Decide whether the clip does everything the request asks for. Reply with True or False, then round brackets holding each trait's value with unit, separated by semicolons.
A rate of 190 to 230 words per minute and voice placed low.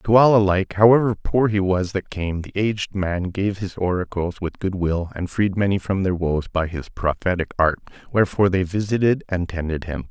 True (200 wpm; 95 Hz)